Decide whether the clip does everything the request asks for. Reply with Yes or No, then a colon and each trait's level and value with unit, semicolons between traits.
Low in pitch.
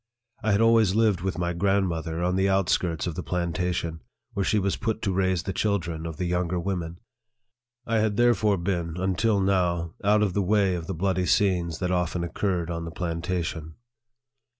Yes: very low, 90 Hz